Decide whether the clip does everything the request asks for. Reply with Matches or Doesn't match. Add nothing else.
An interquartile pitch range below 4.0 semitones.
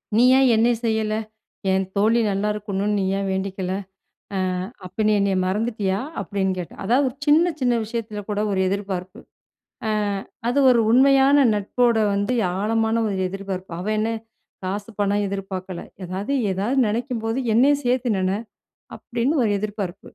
Matches